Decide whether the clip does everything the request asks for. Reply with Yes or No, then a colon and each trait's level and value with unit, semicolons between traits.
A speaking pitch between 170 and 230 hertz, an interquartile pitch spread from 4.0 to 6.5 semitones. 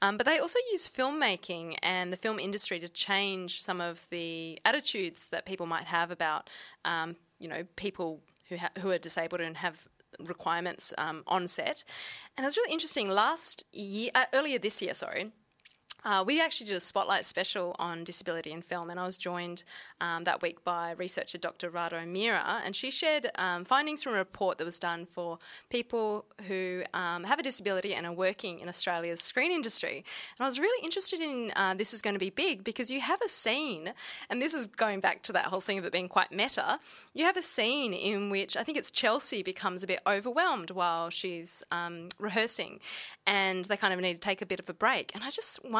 Yes: high, 190 Hz; average, 5.2 semitones